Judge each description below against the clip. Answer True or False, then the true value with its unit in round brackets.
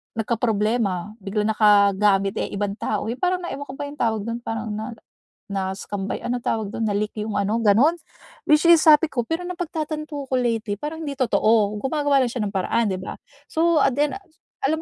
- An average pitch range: False (5.8 semitones)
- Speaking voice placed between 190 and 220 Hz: False (230 Hz)